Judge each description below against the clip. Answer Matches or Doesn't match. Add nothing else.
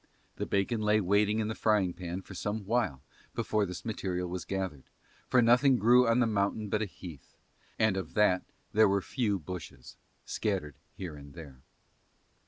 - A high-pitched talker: Doesn't match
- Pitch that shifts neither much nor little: Matches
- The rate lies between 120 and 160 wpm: Doesn't match